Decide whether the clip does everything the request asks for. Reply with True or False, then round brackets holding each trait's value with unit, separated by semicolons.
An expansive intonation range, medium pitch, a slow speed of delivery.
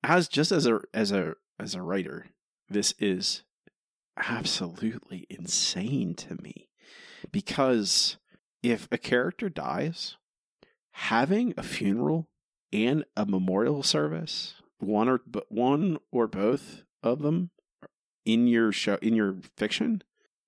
False (7.4 semitones; 120 Hz; 120 wpm)